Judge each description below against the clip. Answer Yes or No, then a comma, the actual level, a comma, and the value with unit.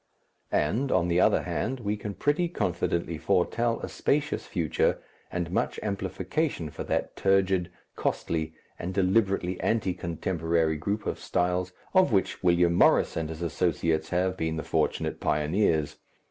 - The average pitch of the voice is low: Yes, very low, 90 Hz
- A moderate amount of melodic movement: Yes, average, 3.4 semitones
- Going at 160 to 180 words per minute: No, average, 145 wpm